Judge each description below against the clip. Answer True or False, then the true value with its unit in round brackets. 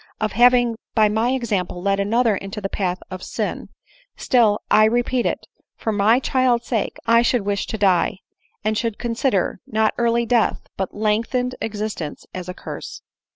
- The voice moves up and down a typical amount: True (3.0 semitones)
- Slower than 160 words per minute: False (170 wpm)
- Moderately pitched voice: False (220 Hz)